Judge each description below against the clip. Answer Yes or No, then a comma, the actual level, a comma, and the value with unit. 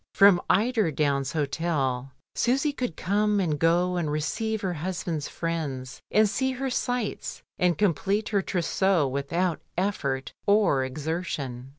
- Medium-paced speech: No, slow, 130 wpm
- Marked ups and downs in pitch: Yes, wide, 5.7 semitones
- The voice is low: No, medium, 175 Hz